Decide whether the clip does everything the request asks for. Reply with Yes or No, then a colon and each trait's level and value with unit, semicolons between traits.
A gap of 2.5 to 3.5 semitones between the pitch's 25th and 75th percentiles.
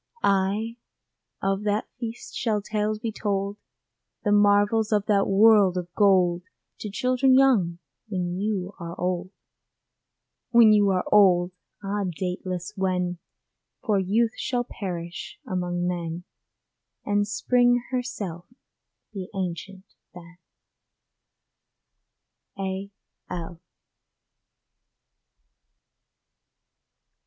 Yes: average, 2.9 semitones